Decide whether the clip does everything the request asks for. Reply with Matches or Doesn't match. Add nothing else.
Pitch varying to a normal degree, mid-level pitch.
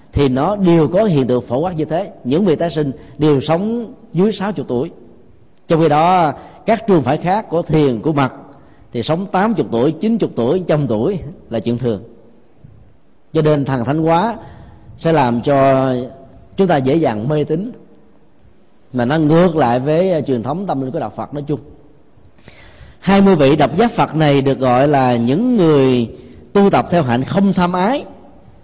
Doesn't match